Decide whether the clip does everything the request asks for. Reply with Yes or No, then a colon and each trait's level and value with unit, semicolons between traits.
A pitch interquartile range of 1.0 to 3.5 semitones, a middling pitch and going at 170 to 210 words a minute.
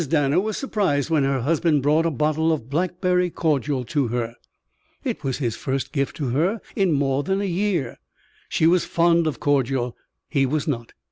No: average, 4.0 semitones; medium, 150 Hz; average, 185 wpm